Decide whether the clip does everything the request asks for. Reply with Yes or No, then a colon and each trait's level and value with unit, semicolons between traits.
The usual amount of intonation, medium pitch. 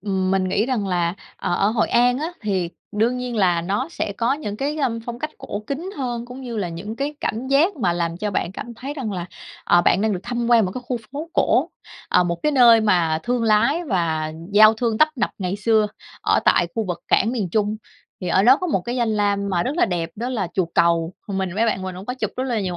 No: average, 5.0 semitones; high, 215 Hz